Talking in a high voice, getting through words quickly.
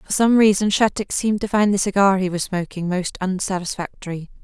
No: high, 195 Hz; average, 190 wpm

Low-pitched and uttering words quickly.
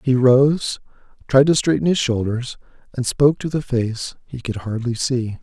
No: low, 125 Hz; average, 175 wpm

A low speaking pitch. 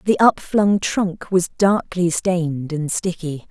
No: medium, 180 Hz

